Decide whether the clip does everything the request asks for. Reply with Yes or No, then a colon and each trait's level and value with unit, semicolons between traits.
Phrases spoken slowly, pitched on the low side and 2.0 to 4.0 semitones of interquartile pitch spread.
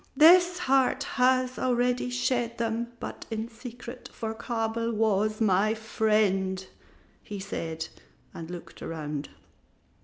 No: slow, 115 wpm; high, 225 Hz; average, 3.5 semitones